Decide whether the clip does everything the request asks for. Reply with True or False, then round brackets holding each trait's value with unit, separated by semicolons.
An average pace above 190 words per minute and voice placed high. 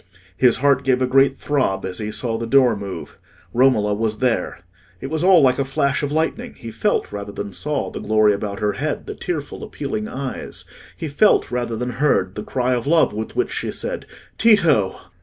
False (200 wpm; 125 Hz)